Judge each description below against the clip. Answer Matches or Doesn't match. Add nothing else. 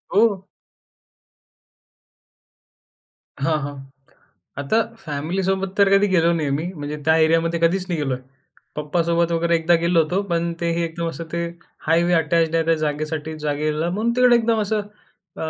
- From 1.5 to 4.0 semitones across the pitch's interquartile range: Matches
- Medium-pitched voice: Matches